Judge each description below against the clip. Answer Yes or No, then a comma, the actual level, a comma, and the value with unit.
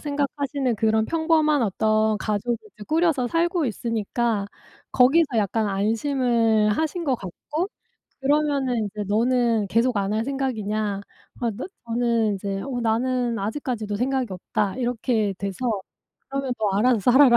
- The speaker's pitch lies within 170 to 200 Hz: No, high, 235 Hz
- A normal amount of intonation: Yes, average, 4.1 semitones